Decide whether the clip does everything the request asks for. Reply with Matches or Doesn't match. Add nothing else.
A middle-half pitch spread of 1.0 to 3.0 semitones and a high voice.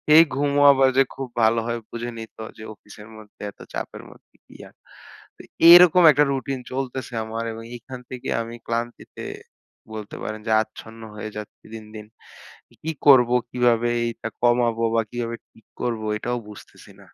Doesn't match